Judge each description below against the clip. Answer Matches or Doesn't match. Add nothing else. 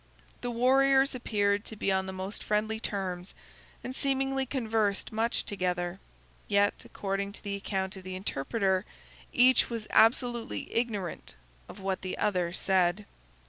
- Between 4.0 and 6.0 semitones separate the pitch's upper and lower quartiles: Doesn't match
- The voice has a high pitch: Matches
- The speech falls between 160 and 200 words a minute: Doesn't match